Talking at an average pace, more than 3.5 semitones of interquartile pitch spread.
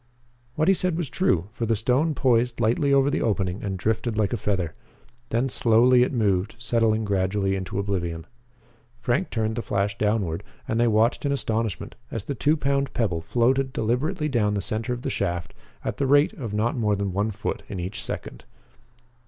Yes: average, 190 wpm; average, 4.1 semitones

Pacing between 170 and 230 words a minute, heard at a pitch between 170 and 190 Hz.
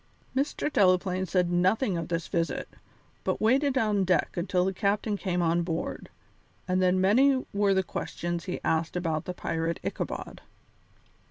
No: average, 155 wpm; medium, 185 Hz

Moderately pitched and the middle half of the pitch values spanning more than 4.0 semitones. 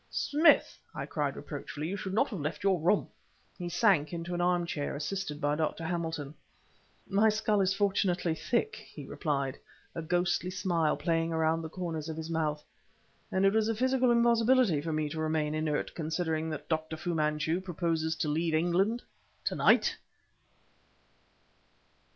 No: medium, 165 Hz; average, 3.4 semitones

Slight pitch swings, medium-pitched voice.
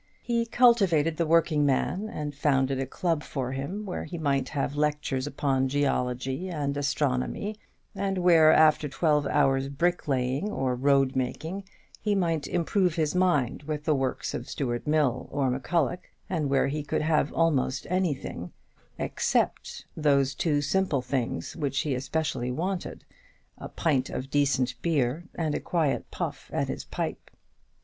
No: average, 3.8 semitones; medium, 145 Hz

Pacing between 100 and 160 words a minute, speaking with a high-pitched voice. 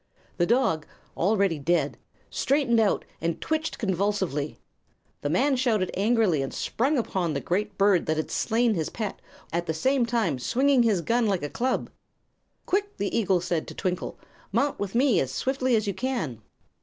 No: average, 170 wpm; high, 205 Hz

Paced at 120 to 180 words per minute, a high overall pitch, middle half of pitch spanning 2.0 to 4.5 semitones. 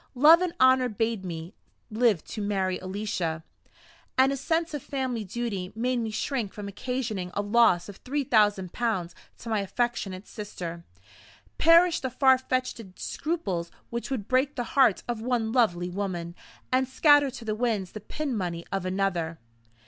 No: average, 165 wpm; high, 225 Hz; average, 5.3 semitones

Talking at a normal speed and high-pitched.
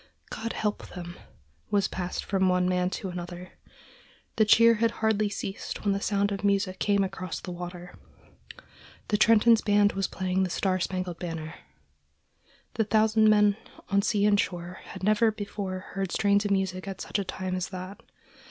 Yes: average, 170 wpm; high, 195 Hz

